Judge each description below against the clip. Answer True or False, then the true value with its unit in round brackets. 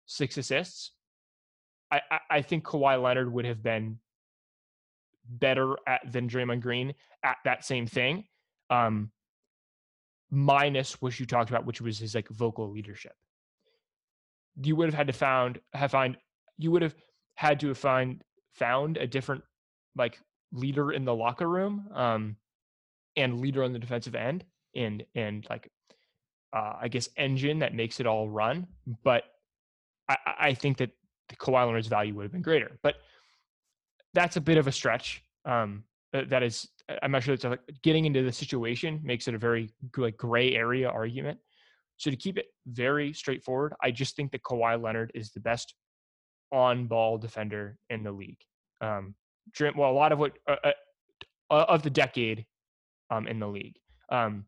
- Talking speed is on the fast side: False (165 wpm)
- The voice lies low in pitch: True (125 Hz)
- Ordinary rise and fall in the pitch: True (4.1 semitones)